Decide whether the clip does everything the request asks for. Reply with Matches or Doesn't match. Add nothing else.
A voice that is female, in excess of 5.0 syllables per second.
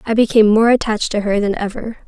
Matches